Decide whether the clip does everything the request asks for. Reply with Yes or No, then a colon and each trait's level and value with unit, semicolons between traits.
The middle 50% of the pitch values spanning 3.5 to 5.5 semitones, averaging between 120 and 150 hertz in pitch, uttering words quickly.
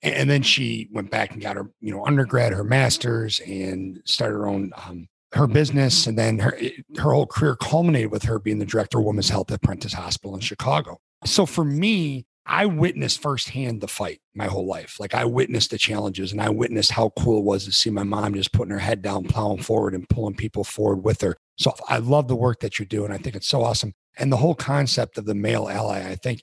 No: average, 4.0 semitones; low, 110 Hz; fast, 235 wpm